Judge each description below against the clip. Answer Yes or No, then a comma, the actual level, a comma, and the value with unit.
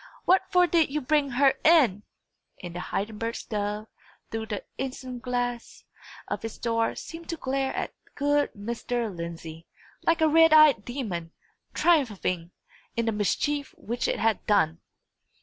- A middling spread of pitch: No, wide, 5.8 semitones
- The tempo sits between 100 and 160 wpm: Yes, average, 145 wpm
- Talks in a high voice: Yes, high, 240 Hz